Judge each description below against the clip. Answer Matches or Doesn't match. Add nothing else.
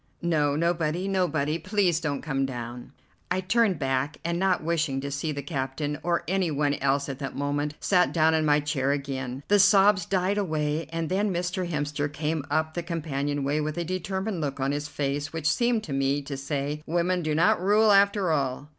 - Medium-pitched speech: Matches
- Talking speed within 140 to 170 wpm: Doesn't match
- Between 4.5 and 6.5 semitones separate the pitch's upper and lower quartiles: Doesn't match